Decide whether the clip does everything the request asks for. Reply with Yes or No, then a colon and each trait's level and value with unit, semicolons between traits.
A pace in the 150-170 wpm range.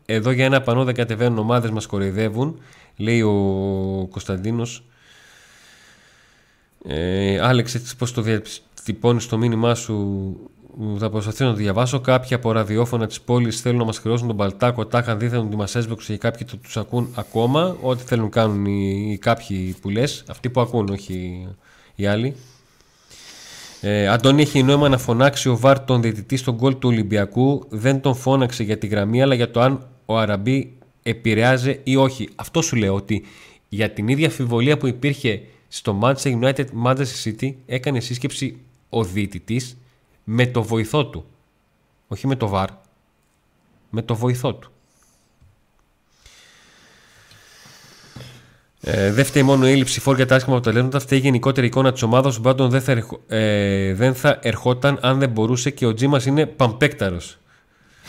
Yes: average, 155 wpm